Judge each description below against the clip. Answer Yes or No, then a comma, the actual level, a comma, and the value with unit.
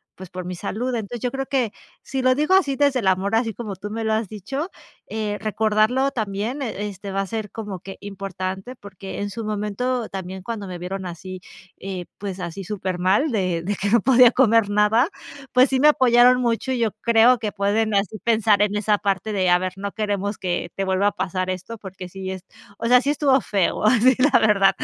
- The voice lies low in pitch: No, high, 210 Hz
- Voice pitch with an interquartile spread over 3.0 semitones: Yes, average, 3.7 semitones